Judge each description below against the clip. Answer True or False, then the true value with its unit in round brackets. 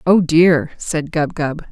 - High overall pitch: False (160 Hz)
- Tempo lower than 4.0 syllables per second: True (3.3 syllables/s)